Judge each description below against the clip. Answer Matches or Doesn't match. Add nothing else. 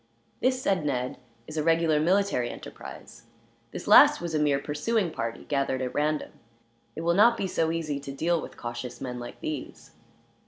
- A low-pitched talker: Doesn't match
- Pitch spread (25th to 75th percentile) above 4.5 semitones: Doesn't match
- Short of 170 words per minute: Doesn't match